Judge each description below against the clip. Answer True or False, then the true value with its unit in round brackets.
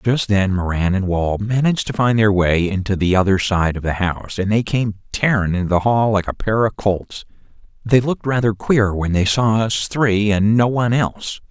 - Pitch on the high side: False (105 Hz)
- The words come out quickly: True (220 wpm)